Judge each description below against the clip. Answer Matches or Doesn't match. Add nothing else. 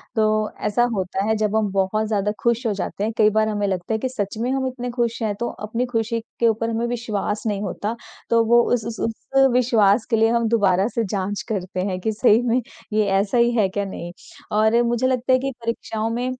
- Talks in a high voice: Matches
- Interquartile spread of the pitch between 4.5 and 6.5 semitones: Doesn't match